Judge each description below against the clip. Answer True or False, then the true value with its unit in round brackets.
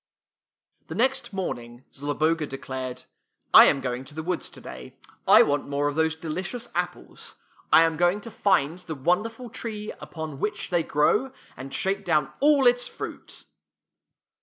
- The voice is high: False (160 Hz)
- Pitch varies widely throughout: True (6.6 semitones)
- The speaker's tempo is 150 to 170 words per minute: True (155 wpm)